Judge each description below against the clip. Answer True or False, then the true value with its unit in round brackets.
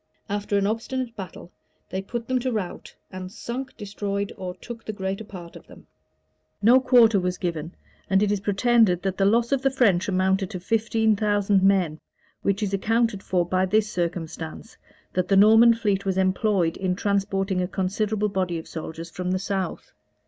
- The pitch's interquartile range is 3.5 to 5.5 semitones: False (2.9 semitones)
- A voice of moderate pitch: False (195 Hz)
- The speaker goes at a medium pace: True (180 wpm)